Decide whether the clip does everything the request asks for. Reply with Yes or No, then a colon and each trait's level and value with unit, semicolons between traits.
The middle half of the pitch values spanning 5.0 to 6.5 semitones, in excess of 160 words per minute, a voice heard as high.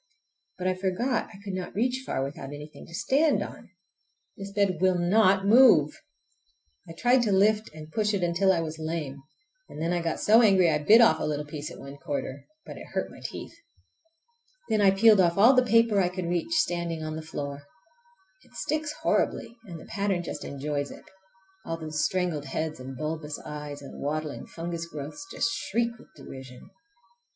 No: wide, 5.4 semitones; average, 190 wpm; medium, 175 Hz